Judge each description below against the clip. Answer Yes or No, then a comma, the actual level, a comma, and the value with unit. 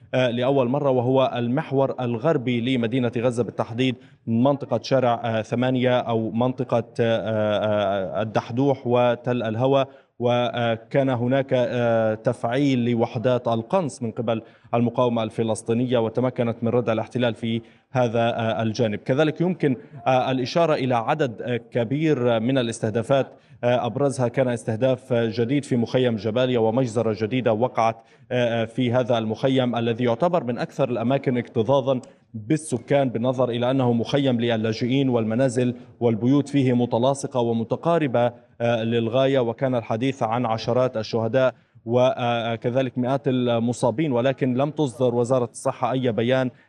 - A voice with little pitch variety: Yes, narrow, 2.1 semitones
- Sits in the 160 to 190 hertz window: No, low, 125 Hz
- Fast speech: No, average, 110 wpm